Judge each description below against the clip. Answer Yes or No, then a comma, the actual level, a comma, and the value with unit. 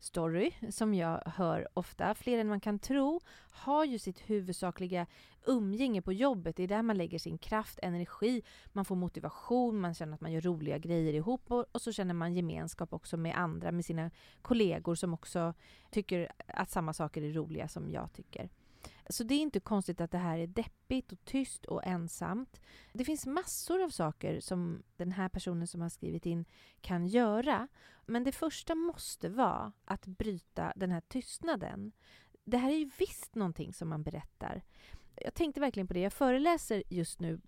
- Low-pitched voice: No, medium, 185 Hz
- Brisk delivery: No, average, 185 wpm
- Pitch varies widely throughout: Yes, wide, 6.0 semitones